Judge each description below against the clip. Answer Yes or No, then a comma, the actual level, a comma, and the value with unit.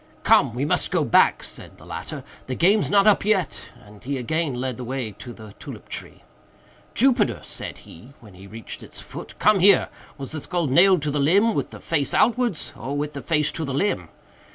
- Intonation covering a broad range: Yes, wide, 7.2 semitones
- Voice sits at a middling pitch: Yes, medium, 150 Hz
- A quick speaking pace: Yes, fast, 210 wpm